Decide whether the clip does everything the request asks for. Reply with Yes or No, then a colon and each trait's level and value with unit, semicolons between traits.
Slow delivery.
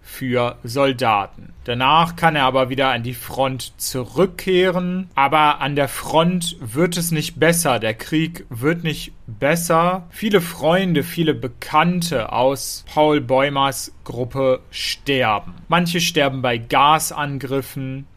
Yes: slow, 120 wpm